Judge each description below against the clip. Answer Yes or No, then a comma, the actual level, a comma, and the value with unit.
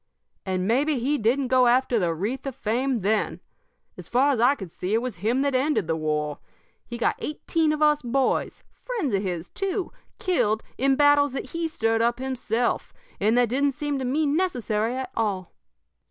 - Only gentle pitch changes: No, average, 4.7 semitones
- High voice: Yes, very high, 250 Hz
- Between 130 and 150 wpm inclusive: No, average, 190 wpm